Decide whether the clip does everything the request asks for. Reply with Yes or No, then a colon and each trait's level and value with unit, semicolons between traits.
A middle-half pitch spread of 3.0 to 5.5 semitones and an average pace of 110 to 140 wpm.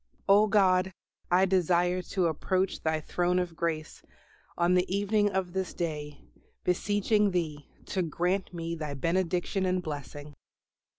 No: narrow, 2.4 semitones; slow, 135 wpm